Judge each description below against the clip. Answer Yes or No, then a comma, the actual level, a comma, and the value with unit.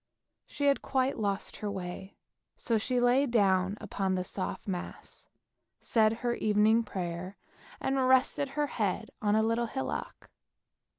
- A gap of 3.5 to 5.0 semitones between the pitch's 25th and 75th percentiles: Yes, average, 4.3 semitones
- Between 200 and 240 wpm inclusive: No, average, 140 wpm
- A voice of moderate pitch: No, high, 215 Hz